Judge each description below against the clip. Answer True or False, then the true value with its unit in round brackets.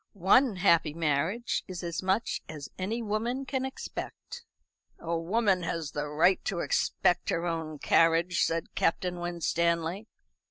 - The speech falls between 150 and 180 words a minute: False (135 wpm)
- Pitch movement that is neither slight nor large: True (3.8 semitones)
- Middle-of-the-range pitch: True (175 Hz)